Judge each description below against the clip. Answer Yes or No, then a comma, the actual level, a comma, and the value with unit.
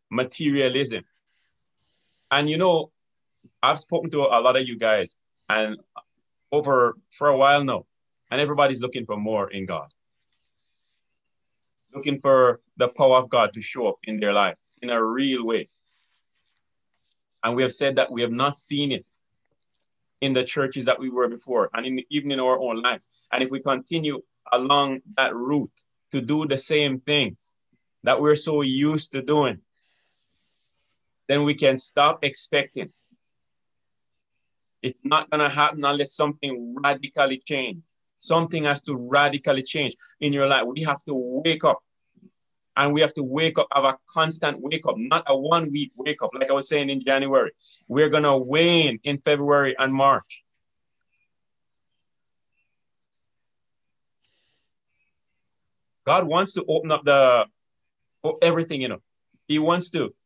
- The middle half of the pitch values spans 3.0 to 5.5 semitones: No, narrow, 2.6 semitones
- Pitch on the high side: No, medium, 140 Hz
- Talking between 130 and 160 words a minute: Yes, average, 150 wpm